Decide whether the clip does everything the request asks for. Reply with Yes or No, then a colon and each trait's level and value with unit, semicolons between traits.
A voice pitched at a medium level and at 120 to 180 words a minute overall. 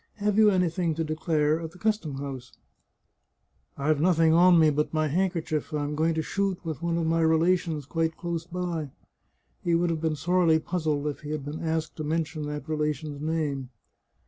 No: medium, 160 Hz; average, 200 wpm